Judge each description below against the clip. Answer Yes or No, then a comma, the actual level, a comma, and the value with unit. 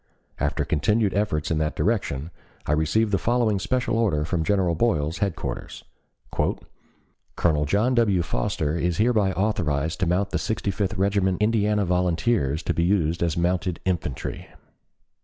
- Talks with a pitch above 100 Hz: No, very low, 90 Hz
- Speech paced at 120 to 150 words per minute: Yes, average, 145 wpm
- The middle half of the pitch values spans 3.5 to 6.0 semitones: Yes, average, 4.6 semitones